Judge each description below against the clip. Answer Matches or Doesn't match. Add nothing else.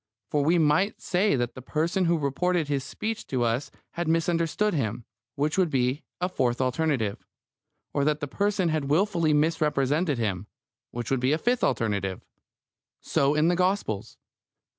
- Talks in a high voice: Doesn't match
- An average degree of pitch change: Matches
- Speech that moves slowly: Doesn't match